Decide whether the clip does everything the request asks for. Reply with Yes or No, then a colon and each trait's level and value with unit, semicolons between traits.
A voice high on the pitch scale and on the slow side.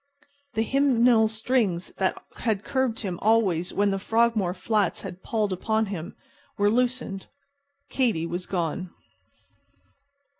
Yes: high, 210 Hz; slow, 120 wpm